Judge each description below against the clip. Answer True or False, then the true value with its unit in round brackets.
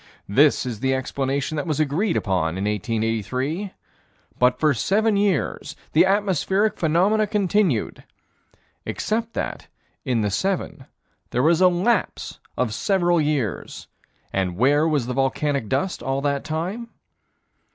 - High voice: False (150 Hz)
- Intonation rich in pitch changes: True (7.0 semitones)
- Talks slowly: True (130 wpm)